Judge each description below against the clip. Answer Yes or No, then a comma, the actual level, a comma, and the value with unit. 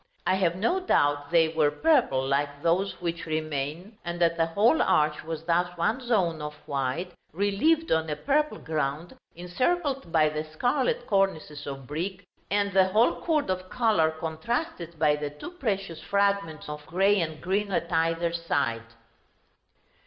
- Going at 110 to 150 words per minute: No, average, 160 wpm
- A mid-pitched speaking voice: Yes, medium, 170 Hz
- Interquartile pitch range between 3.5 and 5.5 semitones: Yes, average, 4.6 semitones